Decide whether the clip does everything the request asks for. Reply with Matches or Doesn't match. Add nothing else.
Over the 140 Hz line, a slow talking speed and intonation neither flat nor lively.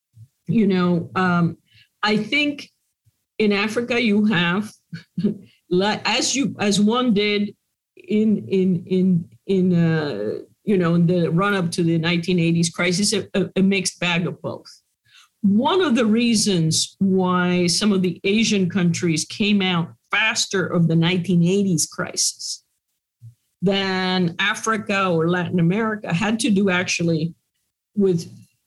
Matches